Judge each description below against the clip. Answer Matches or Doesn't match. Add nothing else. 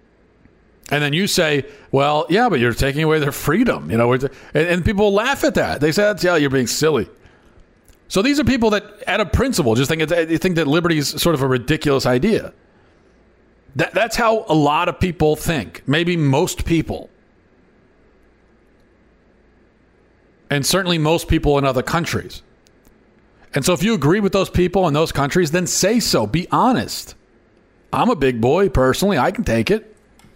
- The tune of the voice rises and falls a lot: Doesn't match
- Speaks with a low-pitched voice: Doesn't match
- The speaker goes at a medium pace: Matches